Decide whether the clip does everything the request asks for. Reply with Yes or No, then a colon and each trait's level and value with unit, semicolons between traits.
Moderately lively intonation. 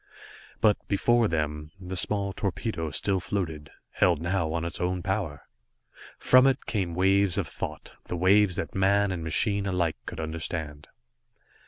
Yes: average, 3.4 semitones